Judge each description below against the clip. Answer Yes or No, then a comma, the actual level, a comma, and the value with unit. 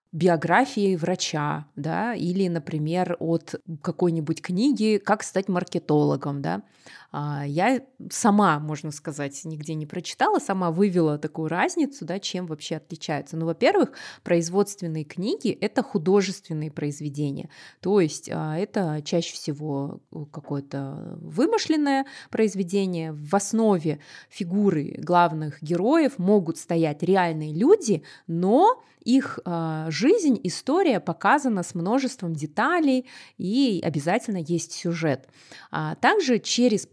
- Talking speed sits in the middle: No, slow, 105 wpm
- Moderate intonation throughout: Yes, average, 4.7 semitones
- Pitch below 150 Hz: No, medium, 175 Hz